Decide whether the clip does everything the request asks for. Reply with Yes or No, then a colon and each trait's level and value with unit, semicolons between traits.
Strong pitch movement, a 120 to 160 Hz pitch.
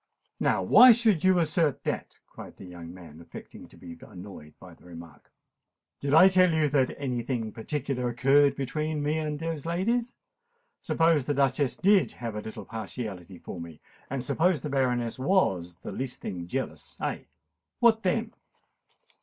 Yes: wide, 7.7 semitones; low, 135 Hz